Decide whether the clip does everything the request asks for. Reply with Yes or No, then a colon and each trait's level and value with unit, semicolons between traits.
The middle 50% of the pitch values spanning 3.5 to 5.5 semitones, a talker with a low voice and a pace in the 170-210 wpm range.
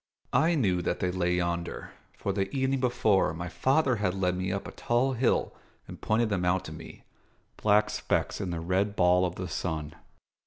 Yes: average, 4.2 semitones; very low, 95 Hz; average, 195 wpm